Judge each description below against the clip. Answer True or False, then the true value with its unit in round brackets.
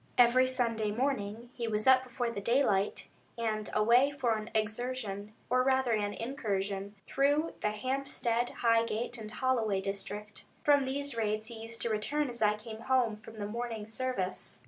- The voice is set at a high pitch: True (230 Hz)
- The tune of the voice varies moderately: True (3.3 semitones)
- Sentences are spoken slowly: False (165 wpm)